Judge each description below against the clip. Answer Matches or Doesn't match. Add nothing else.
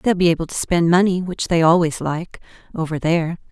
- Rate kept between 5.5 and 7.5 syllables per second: Matches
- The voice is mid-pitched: Matches